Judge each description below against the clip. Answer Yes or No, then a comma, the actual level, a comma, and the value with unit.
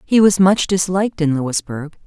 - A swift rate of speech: No, average, 175 wpm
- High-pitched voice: No, medium, 175 Hz